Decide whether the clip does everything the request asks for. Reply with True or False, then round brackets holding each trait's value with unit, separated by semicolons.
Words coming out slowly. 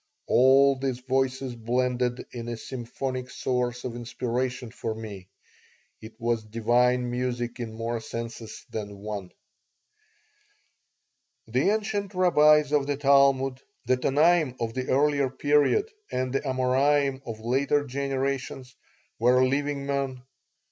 True (120 wpm)